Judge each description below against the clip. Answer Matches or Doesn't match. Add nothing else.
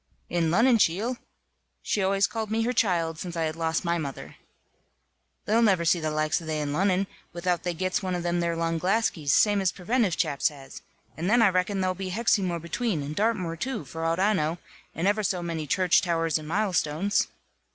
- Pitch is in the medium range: Matches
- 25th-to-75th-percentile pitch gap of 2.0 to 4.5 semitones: Matches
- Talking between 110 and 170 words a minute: Doesn't match